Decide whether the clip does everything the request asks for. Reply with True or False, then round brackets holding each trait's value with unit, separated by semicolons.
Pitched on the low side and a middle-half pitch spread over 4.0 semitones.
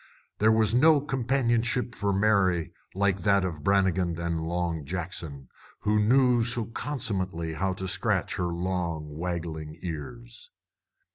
True (95 Hz; 5.0 semitones)